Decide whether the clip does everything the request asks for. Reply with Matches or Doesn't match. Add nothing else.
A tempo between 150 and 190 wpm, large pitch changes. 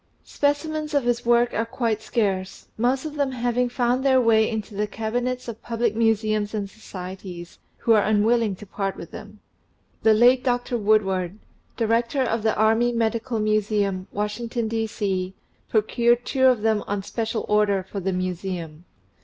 Doesn't match